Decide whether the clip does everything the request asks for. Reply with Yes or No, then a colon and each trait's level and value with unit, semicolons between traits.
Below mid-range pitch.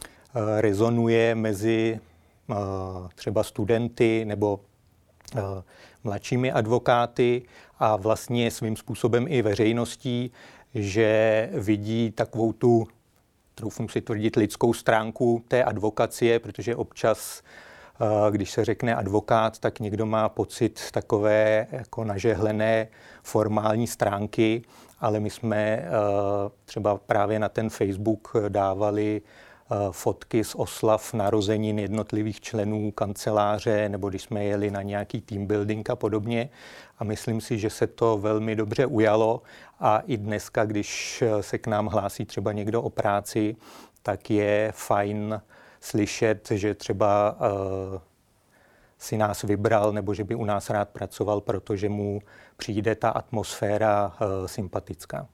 Yes: low, 110 Hz